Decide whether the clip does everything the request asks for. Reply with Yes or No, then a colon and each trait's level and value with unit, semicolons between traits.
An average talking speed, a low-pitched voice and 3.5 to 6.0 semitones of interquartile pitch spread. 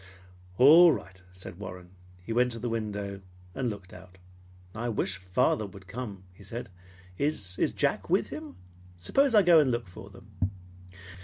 Yes: average, 160 wpm; low, 105 Hz; average, 4.8 semitones